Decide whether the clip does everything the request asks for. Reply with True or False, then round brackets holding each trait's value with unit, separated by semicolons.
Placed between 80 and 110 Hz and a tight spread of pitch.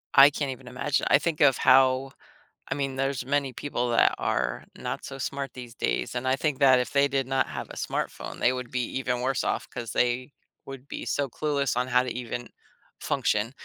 False (130 Hz; 1.8 semitones)